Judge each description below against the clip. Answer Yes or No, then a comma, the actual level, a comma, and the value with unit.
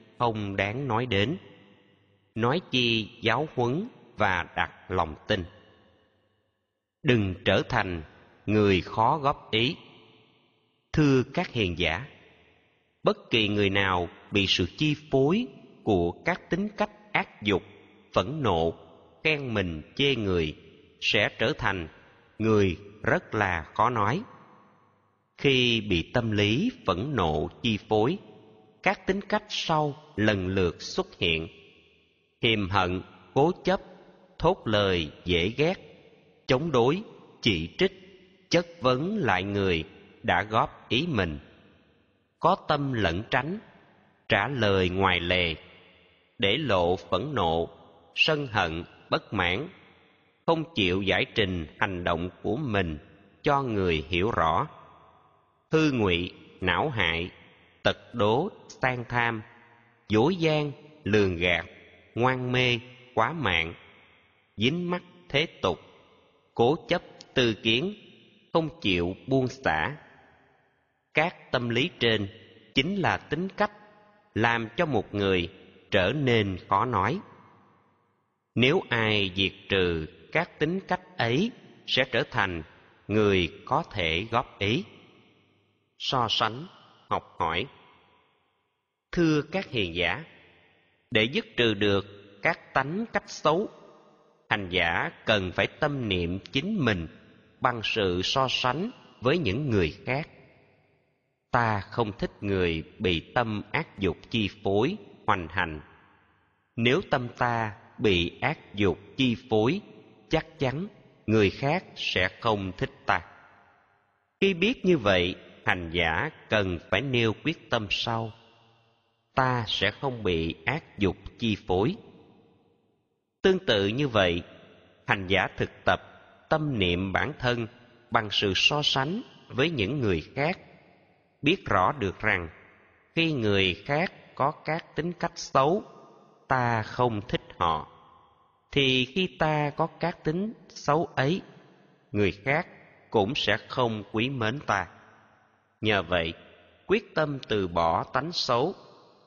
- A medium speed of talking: No, slow, 125 wpm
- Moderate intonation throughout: No, wide, 7.1 semitones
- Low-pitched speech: Yes, low, 110 Hz